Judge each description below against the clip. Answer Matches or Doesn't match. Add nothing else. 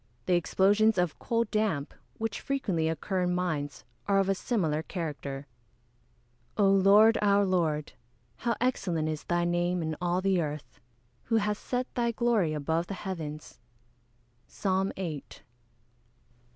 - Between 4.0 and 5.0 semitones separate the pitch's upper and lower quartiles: Matches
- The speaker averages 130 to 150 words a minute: Matches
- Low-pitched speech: Doesn't match